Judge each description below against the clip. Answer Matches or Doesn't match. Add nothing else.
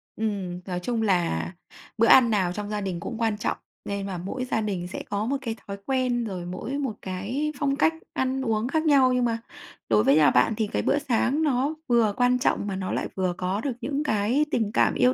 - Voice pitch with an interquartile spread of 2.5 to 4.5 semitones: Doesn't match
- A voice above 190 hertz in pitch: Matches